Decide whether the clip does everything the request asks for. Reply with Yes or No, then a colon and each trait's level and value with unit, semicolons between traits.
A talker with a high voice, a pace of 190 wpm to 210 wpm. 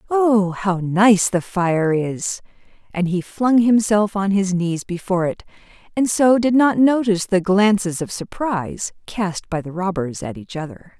No: high, 195 Hz; average, 170 wpm